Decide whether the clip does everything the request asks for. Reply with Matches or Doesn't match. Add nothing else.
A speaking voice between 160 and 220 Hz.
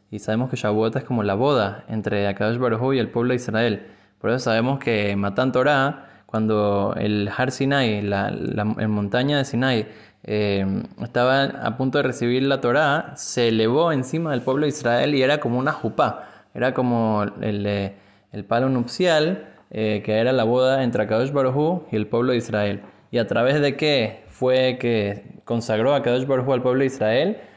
Doesn't match